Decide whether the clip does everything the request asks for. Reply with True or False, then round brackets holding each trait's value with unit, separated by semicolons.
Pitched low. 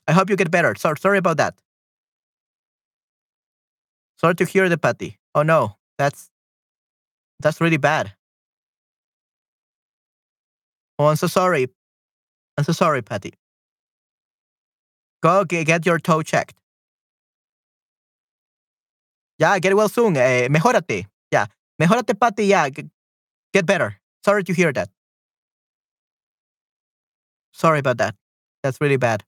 False (165 Hz)